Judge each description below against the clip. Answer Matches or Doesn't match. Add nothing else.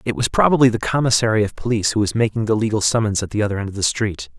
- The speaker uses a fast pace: Matches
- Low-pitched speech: Matches